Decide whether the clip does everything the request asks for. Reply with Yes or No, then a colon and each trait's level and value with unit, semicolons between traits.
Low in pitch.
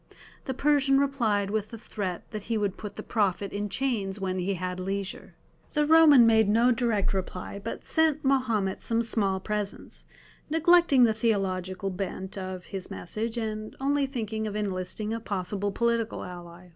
No: high, 215 Hz